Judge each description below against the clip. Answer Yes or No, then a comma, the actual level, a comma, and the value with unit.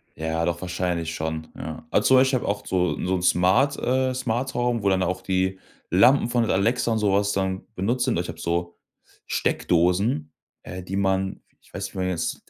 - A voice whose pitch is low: Yes, very low, 95 Hz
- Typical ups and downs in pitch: Yes, average, 4.6 semitones